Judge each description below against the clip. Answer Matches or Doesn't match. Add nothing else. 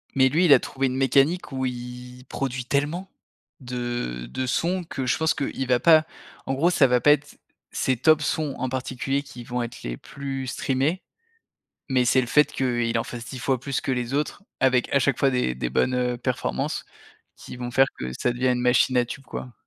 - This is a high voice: Doesn't match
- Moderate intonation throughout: Doesn't match